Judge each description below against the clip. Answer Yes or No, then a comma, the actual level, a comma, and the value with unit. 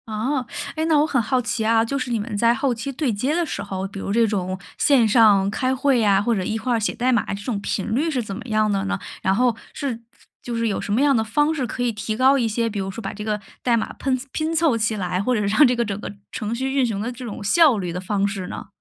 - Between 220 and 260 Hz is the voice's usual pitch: Yes, high, 230 Hz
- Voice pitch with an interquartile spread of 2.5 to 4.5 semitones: Yes, average, 3.9 semitones